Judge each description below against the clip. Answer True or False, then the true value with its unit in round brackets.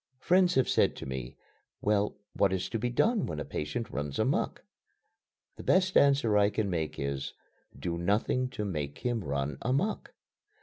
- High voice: False (105 Hz)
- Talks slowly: False (170 wpm)